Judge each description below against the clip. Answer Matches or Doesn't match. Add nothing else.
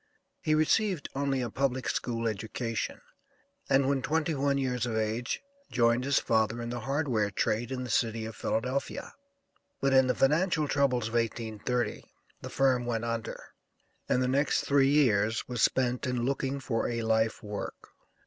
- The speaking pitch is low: Matches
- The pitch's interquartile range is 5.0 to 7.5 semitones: Doesn't match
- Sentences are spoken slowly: Doesn't match